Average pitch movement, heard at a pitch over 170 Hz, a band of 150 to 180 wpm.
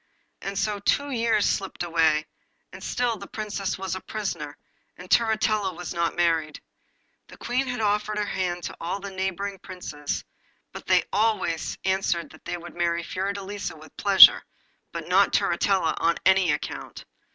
Yes: average, 3.4 semitones; high, 190 Hz; average, 160 wpm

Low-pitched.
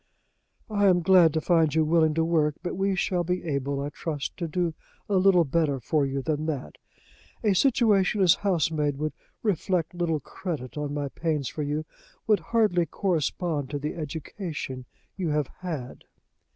No: medium, 160 Hz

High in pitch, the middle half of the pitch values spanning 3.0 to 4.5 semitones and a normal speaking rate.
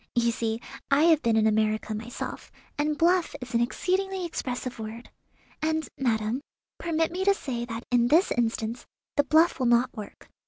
No: very high, 250 Hz; wide, 5.6 semitones; average, 170 wpm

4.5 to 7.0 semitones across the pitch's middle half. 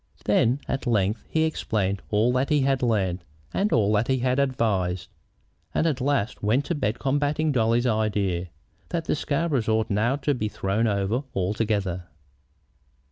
Yes: average, 5.0 semitones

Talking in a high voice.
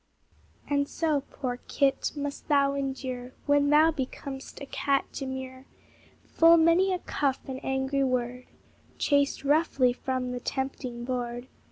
Yes: very high, 270 Hz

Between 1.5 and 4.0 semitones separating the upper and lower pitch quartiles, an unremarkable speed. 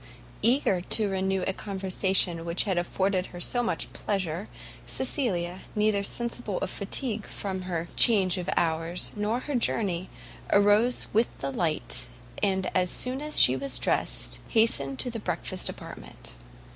Yes: average, 3.7 semitones; average, 145 wpm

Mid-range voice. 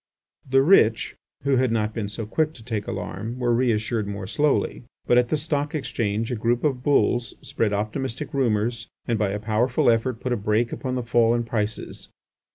No: low, 120 Hz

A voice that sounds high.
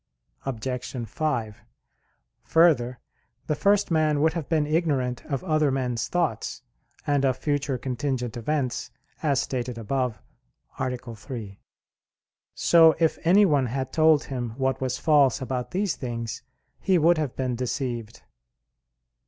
No: low, 135 Hz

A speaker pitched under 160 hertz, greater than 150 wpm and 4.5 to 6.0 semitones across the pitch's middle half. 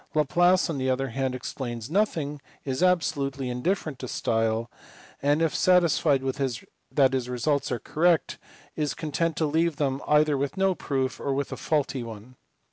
No: medium, 140 Hz; average, 160 wpm; average, 3.6 semitones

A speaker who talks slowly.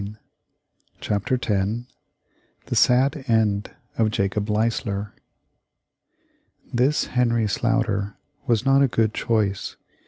Yes: slow, 100 wpm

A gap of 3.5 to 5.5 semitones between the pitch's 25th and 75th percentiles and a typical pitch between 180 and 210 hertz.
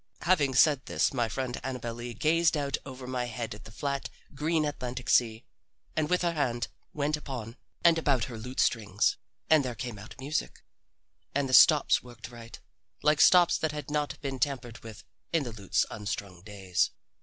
No: average, 4.4 semitones; low, 130 Hz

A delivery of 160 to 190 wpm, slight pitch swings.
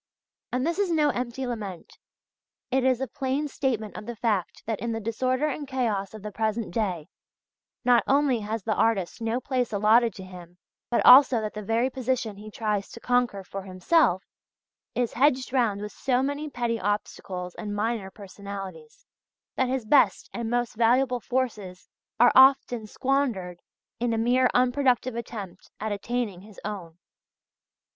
No: average, 165 wpm; average, 3.8 semitones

